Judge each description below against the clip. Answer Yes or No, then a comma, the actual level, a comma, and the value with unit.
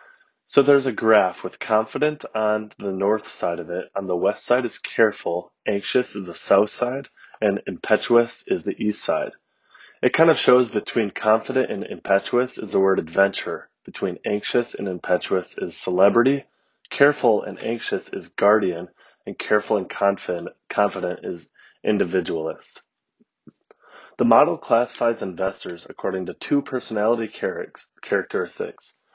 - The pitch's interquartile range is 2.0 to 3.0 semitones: No, average, 4.6 semitones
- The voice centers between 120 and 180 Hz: No, low, 110 Hz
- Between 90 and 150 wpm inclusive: Yes, average, 140 wpm